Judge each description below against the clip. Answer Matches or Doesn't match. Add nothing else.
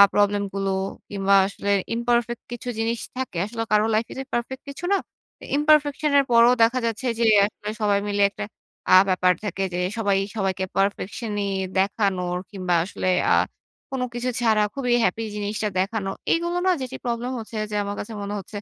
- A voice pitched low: Doesn't match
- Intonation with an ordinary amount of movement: Matches